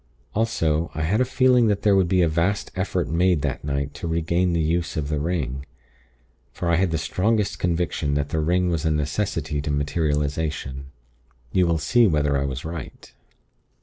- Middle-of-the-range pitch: No, very low, 80 Hz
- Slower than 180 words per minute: No, average, 185 wpm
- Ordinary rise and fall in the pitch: Yes, average, 3.6 semitones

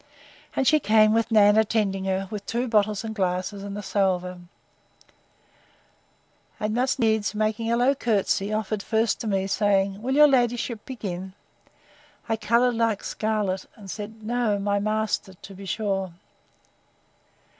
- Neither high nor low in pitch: No, high, 215 Hz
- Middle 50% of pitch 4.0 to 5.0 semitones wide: No, narrow, 2.4 semitones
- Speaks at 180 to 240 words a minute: No, average, 145 wpm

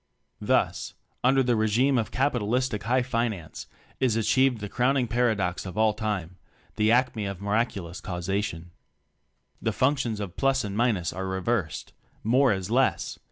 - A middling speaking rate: Yes, average, 150 wpm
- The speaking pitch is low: Yes, low, 110 Hz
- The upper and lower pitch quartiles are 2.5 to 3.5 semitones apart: No, average, 4.2 semitones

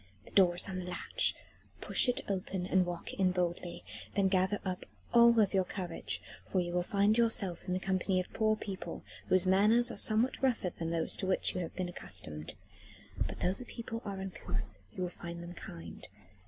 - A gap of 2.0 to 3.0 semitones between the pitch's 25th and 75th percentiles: Yes, narrow, 2.5 semitones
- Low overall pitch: No, medium, 185 Hz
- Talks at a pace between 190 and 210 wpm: Yes, average, 195 wpm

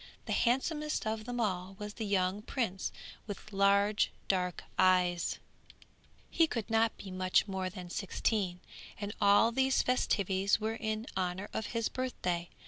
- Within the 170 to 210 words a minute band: No, average, 145 wpm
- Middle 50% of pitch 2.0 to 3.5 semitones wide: Yes, average, 3.2 semitones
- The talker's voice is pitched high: Yes, high, 205 Hz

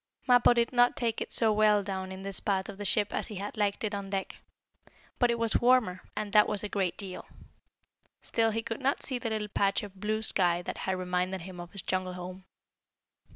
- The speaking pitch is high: Yes, high, 205 Hz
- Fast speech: Yes, fast, 225 wpm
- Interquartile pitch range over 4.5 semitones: No, average, 2.8 semitones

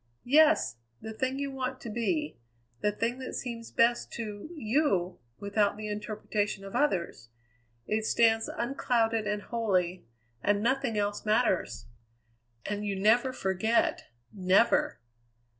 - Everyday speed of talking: No, slow, 125 wpm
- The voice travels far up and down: No, average, 3.1 semitones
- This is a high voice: Yes, high, 220 Hz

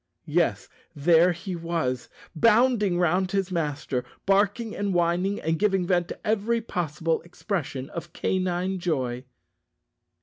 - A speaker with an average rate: No, slow, 125 wpm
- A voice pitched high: No, medium, 175 Hz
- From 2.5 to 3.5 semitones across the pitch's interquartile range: Yes, average, 3.2 semitones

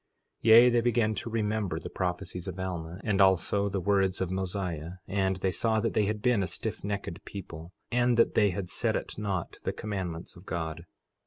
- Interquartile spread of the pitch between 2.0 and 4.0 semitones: Yes, average, 2.9 semitones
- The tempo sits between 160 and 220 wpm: Yes, average, 195 wpm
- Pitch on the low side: Yes, very low, 95 Hz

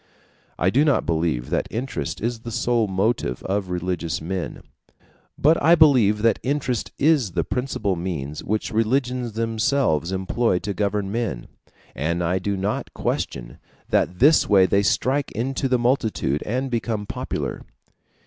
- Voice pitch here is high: No, low, 105 Hz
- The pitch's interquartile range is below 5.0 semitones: No, average, 5.3 semitones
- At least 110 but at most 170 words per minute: Yes, average, 150 wpm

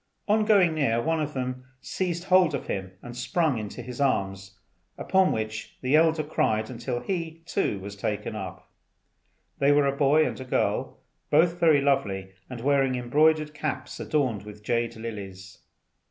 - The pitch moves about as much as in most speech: No, wide, 6.3 semitones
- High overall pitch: No, low, 130 Hz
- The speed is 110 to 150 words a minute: No, average, 160 wpm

